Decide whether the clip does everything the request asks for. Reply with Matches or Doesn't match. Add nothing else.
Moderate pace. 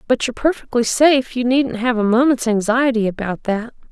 Matches